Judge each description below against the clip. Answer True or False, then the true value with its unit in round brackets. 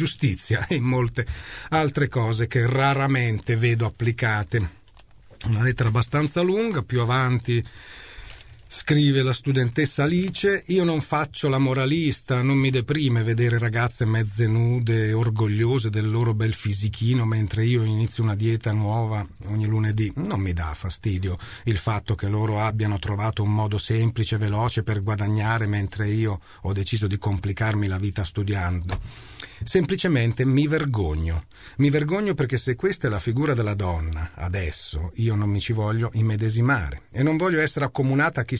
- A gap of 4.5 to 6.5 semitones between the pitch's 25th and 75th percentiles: False (3.8 semitones)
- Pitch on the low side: True (115 Hz)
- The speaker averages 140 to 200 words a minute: True (150 wpm)